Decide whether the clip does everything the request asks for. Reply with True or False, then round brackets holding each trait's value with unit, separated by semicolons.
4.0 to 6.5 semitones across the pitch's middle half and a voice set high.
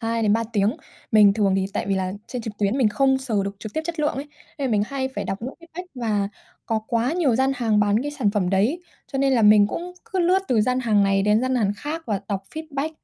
True (4.9 semitones; 230 Hz)